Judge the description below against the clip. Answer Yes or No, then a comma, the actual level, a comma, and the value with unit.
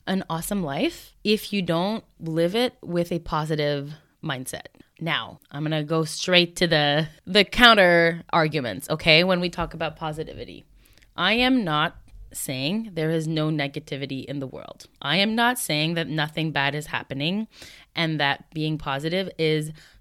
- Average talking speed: Yes, average, 160 wpm